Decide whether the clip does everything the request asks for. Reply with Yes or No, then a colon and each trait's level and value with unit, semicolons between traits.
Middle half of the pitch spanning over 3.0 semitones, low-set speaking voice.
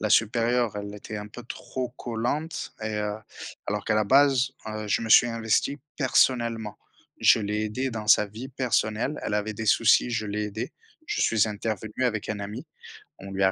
No: narrow, 2.6 semitones; low, 110 Hz